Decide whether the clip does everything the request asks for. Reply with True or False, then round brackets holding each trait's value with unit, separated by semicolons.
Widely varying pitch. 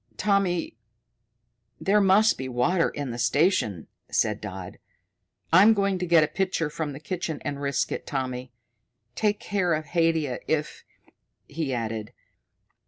True (6.4 semitones)